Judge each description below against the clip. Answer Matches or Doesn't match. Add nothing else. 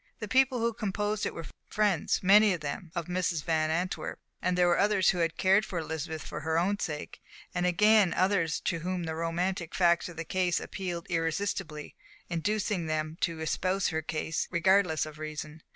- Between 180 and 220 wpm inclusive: Matches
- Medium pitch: Matches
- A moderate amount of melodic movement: Matches